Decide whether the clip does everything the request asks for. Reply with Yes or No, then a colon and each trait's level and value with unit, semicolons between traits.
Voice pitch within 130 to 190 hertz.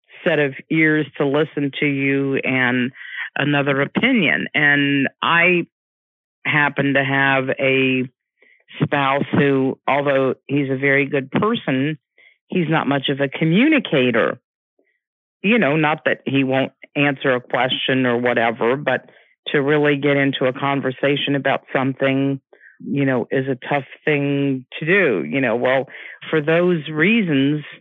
Yes: medium, 140 Hz